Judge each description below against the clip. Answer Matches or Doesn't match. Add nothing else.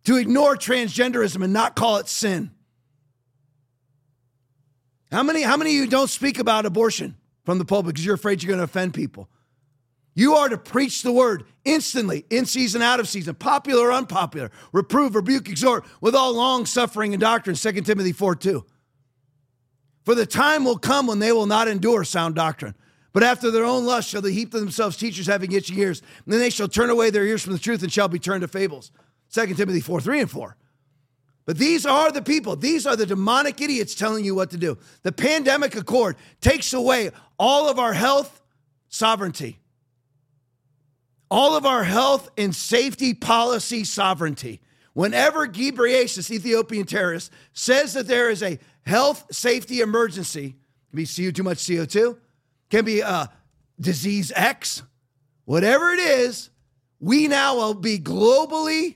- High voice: Matches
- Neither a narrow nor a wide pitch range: Doesn't match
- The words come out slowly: Doesn't match